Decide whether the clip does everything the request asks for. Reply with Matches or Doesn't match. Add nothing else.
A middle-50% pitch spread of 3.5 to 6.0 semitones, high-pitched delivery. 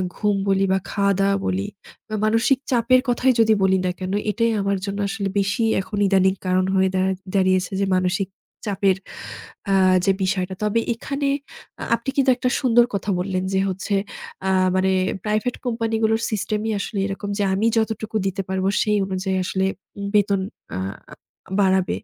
Doesn't match